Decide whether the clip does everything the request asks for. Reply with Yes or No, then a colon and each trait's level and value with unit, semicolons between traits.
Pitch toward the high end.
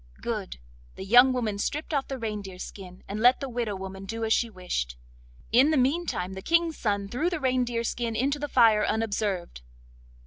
Yes: high, 225 Hz